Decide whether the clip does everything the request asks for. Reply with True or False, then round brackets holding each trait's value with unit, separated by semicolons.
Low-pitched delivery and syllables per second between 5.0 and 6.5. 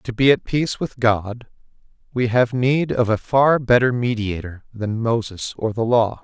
False (120 Hz; 4.4 syllables/s)